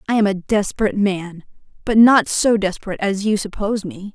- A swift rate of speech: No, average, 190 wpm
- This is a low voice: No, high, 205 Hz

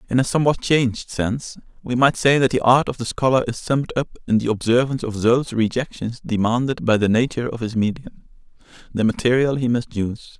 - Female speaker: No, male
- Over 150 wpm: Yes, average, 200 wpm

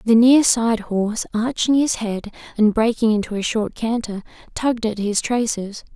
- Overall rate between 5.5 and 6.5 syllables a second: No, 4.7 syllables/s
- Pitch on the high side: Yes, high, 220 Hz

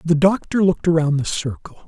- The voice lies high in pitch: No, medium, 165 Hz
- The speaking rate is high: No, average, 190 wpm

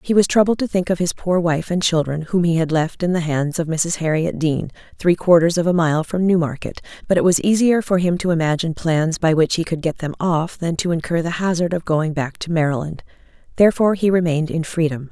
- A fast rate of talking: Yes, fast, 240 wpm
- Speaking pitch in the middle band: Yes, medium, 170 Hz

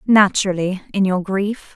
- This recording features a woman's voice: Yes, female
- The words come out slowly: Yes, slow, 105 wpm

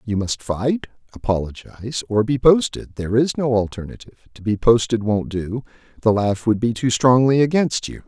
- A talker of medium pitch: No, low, 115 Hz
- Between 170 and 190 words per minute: Yes, average, 180 wpm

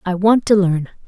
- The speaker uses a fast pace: Yes, fast, 225 wpm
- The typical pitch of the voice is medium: No, high, 195 Hz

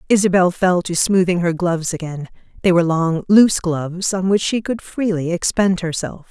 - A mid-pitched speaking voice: Yes, medium, 180 Hz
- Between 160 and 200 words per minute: Yes, average, 180 wpm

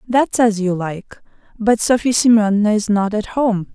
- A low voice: No, high, 215 Hz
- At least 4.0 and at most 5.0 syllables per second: Yes, 4.6 syllables/s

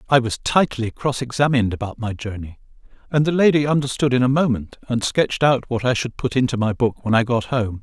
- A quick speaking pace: Yes, fast, 220 wpm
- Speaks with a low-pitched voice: Yes, low, 125 Hz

